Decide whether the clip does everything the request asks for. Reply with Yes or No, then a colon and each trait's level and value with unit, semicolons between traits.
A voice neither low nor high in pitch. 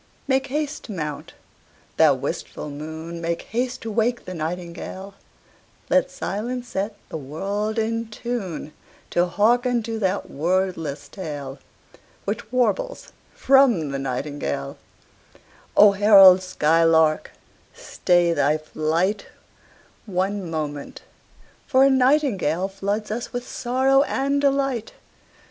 No: high, 195 Hz